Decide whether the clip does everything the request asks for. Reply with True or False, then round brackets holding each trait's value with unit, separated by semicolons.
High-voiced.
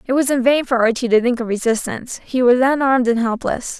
True (245 Hz)